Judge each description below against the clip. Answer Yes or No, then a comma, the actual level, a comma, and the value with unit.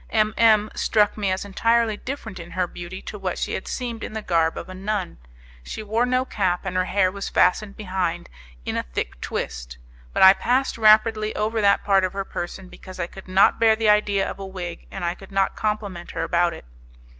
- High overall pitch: Yes, high, 195 Hz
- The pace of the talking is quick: Yes, fast, 220 wpm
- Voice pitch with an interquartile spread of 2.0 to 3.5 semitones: Yes, average, 2.8 semitones